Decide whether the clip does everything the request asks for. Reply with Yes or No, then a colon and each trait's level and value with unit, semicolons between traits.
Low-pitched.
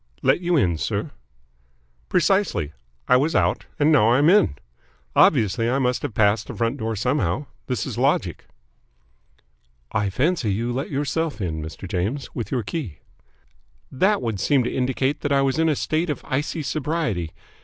Yes: low, 130 Hz